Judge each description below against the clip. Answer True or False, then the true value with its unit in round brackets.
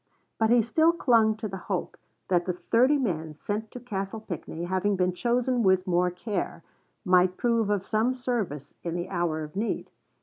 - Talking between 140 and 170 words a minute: False (180 wpm)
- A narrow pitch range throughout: False (4.6 semitones)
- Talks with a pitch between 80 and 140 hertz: False (195 Hz)